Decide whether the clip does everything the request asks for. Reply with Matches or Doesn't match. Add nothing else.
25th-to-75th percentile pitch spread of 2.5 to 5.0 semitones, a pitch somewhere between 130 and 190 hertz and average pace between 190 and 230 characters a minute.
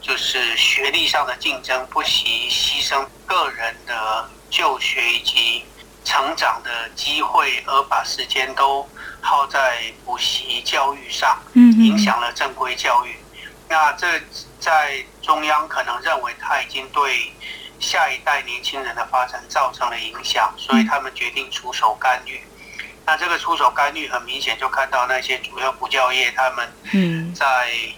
Matches